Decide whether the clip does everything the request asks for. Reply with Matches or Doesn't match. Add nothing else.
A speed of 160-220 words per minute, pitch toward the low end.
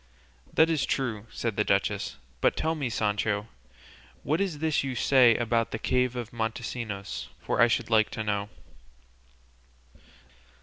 Doesn't match